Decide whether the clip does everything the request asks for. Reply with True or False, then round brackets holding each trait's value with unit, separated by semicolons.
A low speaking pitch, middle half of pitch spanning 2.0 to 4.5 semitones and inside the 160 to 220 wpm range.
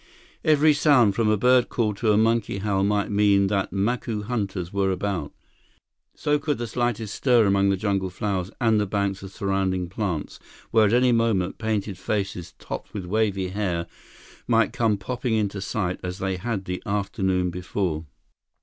True (100 Hz; 2.9 semitones; 170 wpm)